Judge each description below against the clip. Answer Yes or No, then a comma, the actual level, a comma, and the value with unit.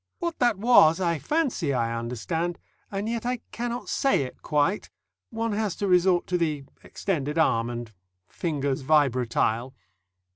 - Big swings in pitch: Yes, wide, 8.1 semitones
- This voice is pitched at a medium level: Yes, medium, 170 Hz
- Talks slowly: No, average, 145 wpm